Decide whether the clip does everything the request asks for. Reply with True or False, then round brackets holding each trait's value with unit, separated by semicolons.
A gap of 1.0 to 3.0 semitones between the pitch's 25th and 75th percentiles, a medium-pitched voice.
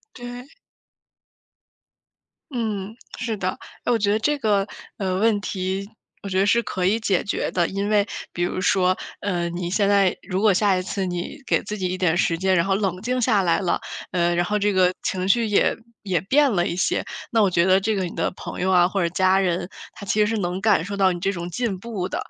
False (2.5 semitones; 195 Hz)